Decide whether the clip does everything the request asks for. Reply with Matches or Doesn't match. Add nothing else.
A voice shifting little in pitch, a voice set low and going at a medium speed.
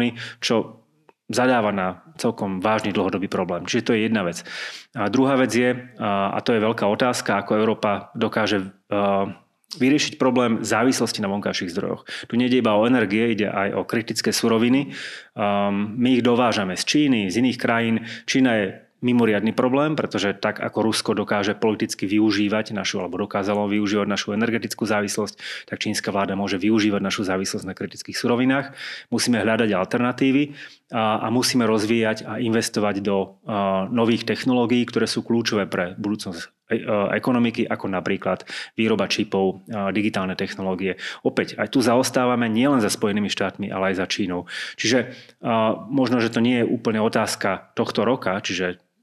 Doesn't match